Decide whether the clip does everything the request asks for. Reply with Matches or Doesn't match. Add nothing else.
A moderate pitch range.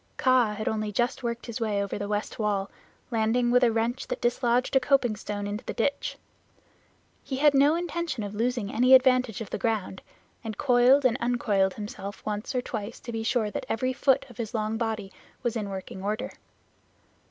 Matches